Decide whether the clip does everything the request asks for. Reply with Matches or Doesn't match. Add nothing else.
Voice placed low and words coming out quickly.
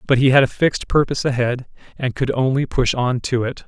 Matches